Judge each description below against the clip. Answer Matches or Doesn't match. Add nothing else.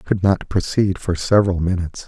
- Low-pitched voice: Matches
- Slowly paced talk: Doesn't match